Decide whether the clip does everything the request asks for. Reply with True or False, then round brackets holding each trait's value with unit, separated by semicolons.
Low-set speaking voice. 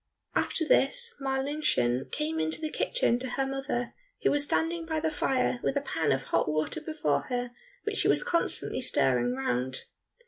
False (270 Hz)